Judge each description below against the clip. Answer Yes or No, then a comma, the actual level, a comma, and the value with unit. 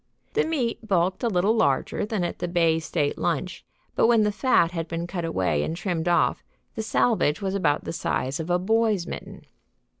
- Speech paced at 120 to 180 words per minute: No, average, 200 wpm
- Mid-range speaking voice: Yes, medium, 180 Hz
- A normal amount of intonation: Yes, average, 4.6 semitones